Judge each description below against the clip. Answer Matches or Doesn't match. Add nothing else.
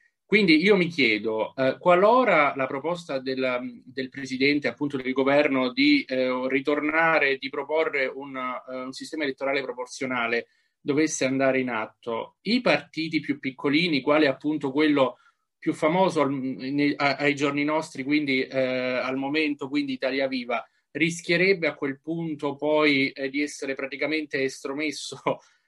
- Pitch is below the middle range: Doesn't match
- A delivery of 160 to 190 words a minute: Doesn't match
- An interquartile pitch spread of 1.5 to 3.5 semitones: Matches